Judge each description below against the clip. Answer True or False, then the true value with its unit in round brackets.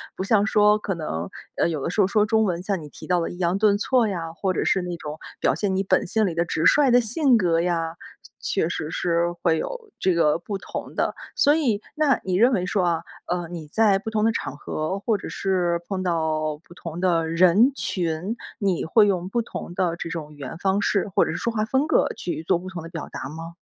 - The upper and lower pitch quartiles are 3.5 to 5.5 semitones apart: True (4.0 semitones)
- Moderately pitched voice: True (180 Hz)